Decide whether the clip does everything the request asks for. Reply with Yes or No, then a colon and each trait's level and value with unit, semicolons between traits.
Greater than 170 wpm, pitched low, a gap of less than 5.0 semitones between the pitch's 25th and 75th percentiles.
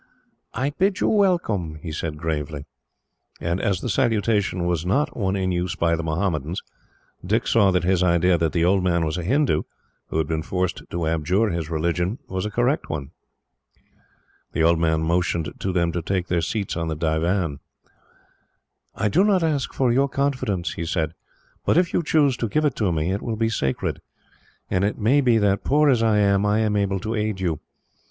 No: average, 200 wpm; very low, 95 Hz; average, 5.3 semitones